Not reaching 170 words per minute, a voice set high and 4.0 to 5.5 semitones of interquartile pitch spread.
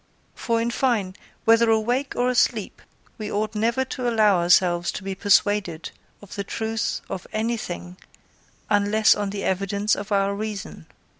No: average, 150 wpm; high, 210 Hz; narrow, 2.5 semitones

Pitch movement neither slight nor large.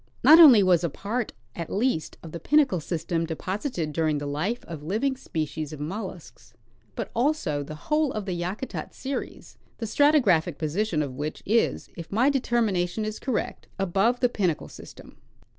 No: wide, 7.0 semitones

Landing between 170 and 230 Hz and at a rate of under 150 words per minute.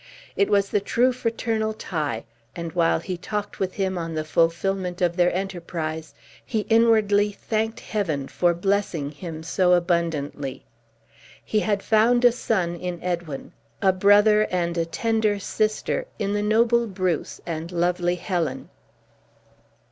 Yes: medium, 185 Hz; average, 140 wpm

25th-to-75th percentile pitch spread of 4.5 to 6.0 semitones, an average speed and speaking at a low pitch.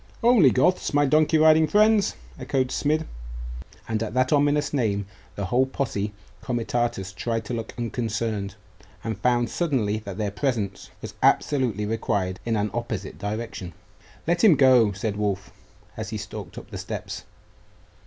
Yes: average, 5.3 semitones; average, 150 wpm; low, 115 Hz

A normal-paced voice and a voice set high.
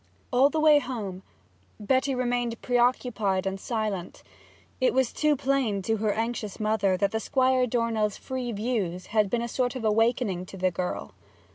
Yes: average, 160 wpm; high, 225 Hz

